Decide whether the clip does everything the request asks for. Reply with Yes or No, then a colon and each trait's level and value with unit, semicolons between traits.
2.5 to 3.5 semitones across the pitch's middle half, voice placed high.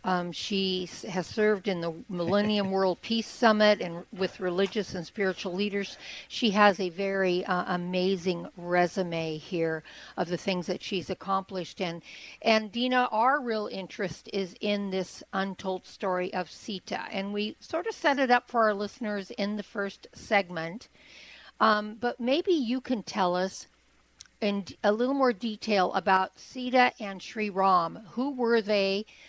Yes: average, 2.9 semitones; high, 195 Hz